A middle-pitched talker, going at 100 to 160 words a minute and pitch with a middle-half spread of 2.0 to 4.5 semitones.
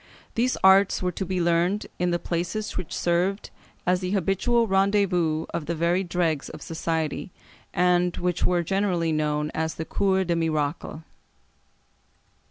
Yes: medium, 175 Hz; average, 150 wpm; narrow, 2.6 semitones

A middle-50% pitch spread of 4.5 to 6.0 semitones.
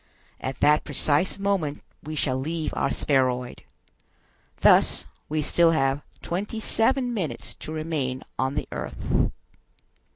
No: average, 4.1 semitones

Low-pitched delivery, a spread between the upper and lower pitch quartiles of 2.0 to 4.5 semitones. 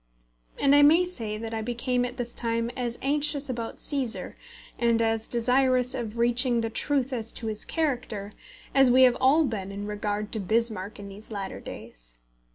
No: high, 235 Hz; average, 3.1 semitones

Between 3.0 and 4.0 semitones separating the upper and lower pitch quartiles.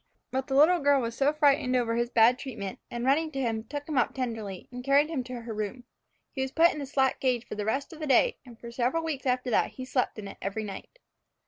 Yes: average, 3.3 semitones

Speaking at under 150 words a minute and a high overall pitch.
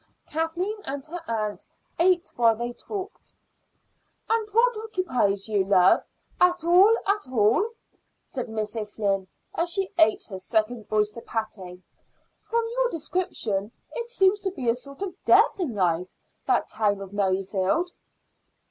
Yes: average, 140 wpm; high, 245 Hz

